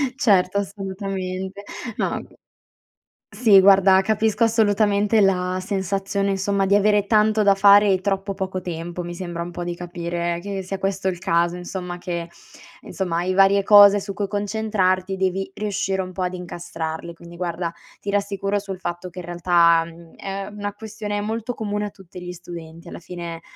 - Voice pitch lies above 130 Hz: Yes, high, 190 Hz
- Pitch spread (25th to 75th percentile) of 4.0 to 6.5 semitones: No, narrow, 2.4 semitones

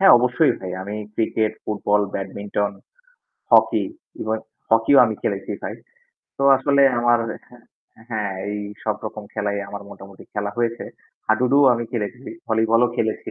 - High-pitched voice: No, low, 110 Hz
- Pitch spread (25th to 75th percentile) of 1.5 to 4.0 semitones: Yes, narrow, 2.6 semitones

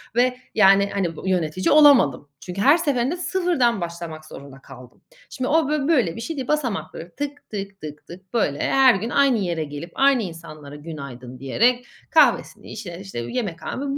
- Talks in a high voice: Yes, high, 195 Hz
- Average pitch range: No, wide, 8.6 semitones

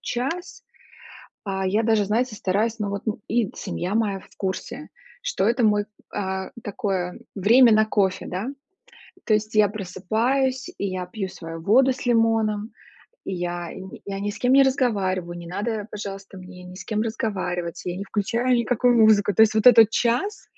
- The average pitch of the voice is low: No, high, 210 Hz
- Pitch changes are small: No, average, 3.4 semitones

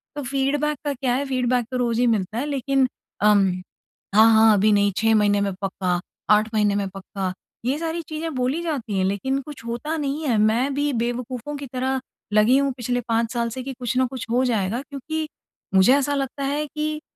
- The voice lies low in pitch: No, very high, 250 Hz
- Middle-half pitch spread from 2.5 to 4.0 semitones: No, average, 4.4 semitones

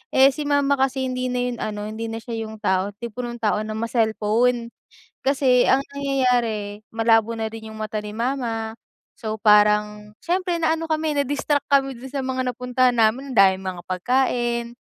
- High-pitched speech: Yes, high, 235 Hz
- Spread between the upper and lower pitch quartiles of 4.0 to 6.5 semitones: No, average, 3.4 semitones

